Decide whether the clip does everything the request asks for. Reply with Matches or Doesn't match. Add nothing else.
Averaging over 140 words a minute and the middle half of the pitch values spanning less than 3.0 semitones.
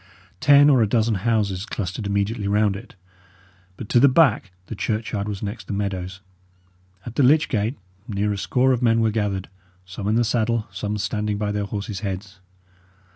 Matches